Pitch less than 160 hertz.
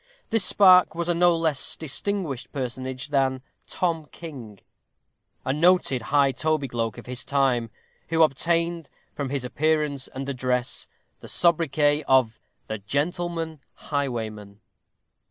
Yes: medium, 140 Hz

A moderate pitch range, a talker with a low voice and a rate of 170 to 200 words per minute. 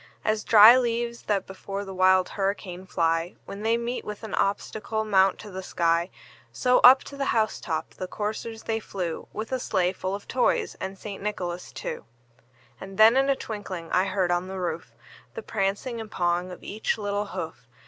No: average, 3.1 semitones; high, 200 Hz; average, 190 wpm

